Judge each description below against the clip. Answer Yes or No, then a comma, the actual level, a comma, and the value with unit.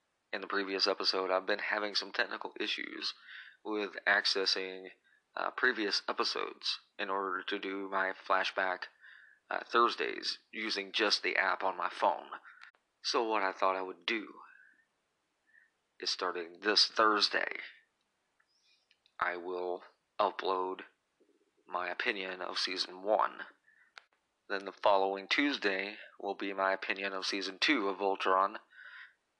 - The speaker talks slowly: Yes, slow, 125 wpm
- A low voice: Yes, very low, 95 Hz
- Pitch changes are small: Yes, narrow, 1.0 semitones